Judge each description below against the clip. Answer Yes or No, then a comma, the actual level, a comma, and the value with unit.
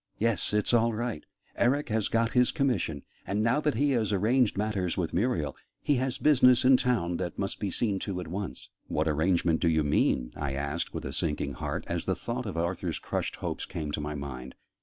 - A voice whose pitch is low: Yes, low, 100 Hz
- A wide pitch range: Yes, wide, 7.0 semitones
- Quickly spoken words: Yes, fast, 210 wpm